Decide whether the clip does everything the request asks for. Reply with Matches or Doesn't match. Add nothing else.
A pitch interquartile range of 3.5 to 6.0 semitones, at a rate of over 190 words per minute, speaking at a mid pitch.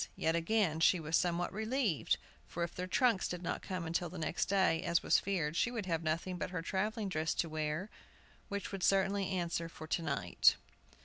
Doesn't match